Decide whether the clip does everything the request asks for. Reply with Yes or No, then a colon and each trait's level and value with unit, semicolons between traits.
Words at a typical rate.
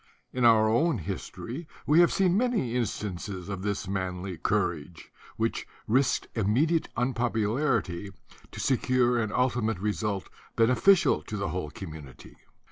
No: slow, 130 wpm